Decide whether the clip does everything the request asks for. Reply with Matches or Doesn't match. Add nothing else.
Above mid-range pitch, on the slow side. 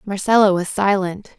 Matches